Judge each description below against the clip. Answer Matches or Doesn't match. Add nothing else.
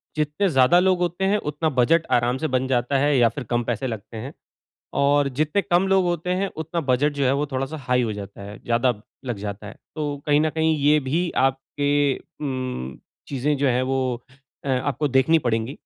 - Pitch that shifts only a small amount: Doesn't match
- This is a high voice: Doesn't match